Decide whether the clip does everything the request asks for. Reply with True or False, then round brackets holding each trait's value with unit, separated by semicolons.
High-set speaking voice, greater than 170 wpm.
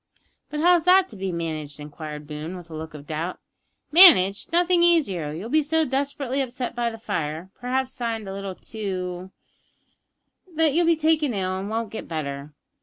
True (210 Hz; 180 wpm)